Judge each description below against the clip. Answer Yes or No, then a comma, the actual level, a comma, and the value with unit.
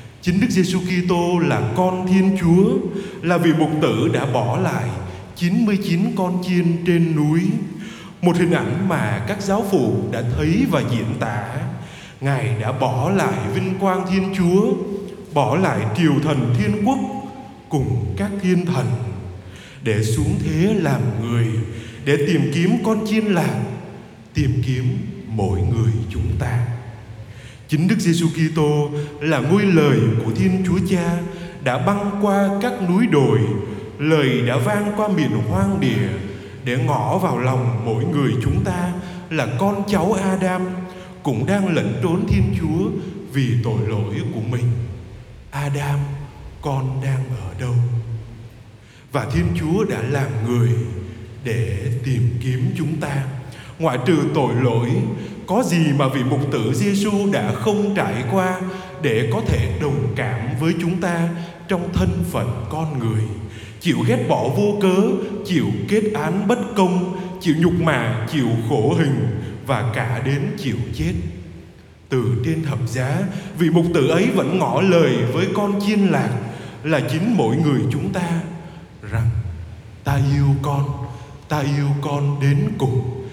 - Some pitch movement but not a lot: No, wide, 7.1 semitones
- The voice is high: No, medium, 145 Hz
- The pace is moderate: No, slow, 150 wpm